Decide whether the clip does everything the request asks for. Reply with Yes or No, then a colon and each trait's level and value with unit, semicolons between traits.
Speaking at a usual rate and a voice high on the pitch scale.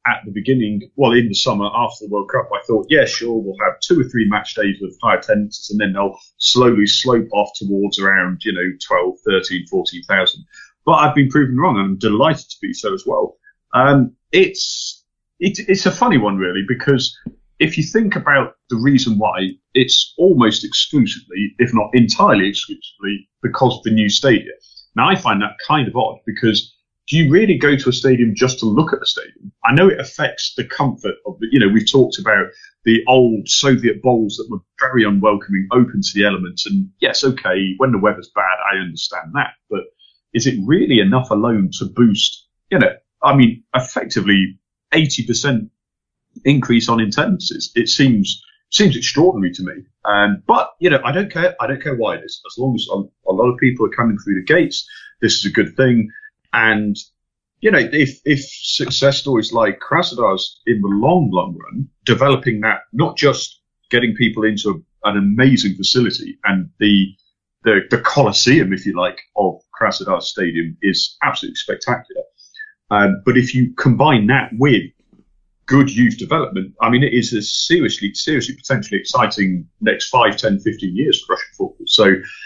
No: average, 185 wpm; low, 125 Hz